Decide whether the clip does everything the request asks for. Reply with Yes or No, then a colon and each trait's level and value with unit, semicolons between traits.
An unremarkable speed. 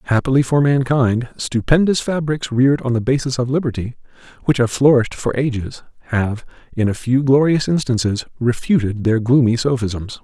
Yes: average, 150 wpm